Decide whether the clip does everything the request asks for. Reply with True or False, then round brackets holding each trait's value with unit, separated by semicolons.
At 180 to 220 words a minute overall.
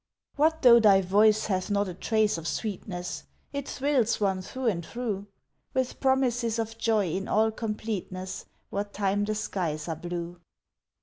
False (160 wpm)